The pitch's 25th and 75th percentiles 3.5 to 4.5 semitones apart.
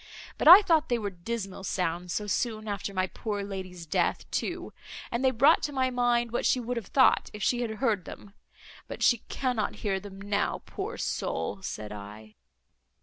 Yes: average, 4.1 semitones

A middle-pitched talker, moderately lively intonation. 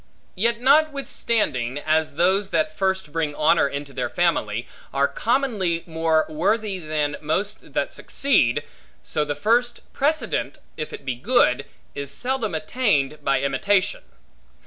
No: medium, 165 Hz; wide, 7.0 semitones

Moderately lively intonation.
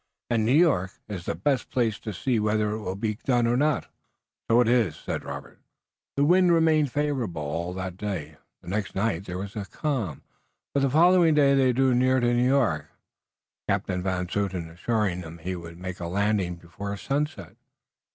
No: wide, 6.4 semitones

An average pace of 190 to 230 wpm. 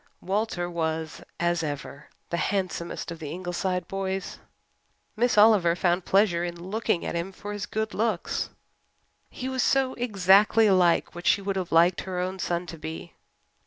No: average, 160 wpm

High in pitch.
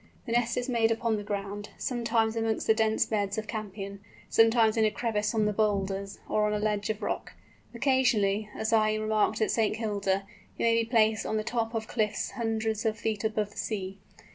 Yes: high, 215 Hz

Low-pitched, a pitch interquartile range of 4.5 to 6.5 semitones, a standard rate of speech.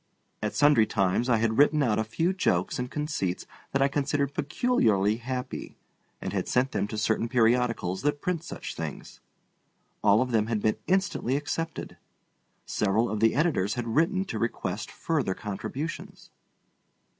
Yes: low, 125 Hz; average, 5.2 semitones; average, 155 wpm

